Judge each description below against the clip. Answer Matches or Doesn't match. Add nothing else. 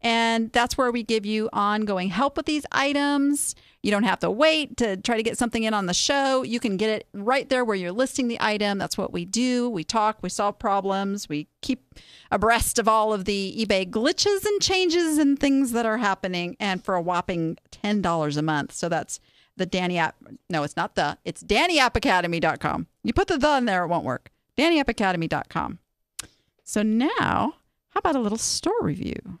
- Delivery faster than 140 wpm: Matches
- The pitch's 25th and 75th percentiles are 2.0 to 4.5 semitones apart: Doesn't match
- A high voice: Matches